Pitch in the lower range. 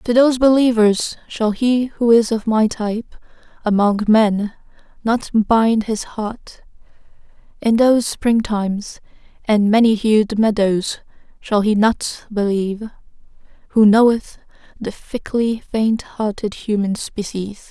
No: high, 220 Hz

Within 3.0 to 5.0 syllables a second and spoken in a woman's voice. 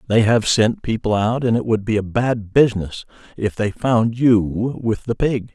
No: 4.4 syllables/s; male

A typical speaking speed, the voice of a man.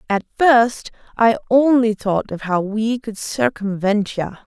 No: average, 145 wpm; female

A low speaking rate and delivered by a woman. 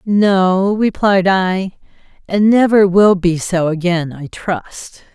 Yes: slow, 130 wpm; female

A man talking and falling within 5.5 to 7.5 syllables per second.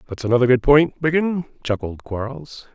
No: male; 5.3 syllables/s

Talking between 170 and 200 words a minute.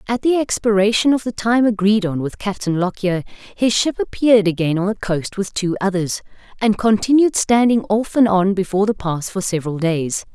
Yes: average, 190 wpm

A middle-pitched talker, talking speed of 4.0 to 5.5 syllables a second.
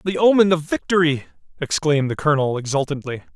No: medium, 155 Hz; 6.5 syllables/s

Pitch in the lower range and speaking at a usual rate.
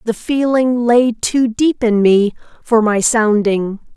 No: high, 230 Hz; average, 150 wpm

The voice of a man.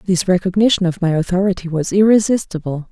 No: female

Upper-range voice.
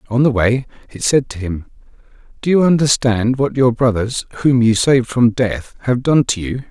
No: low, 120 Hz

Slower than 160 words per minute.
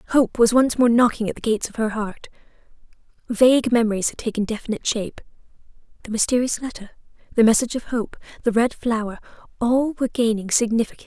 No: average, 165 wpm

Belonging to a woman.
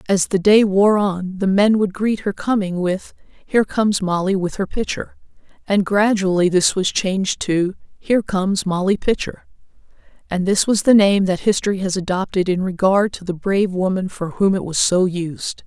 Yes: female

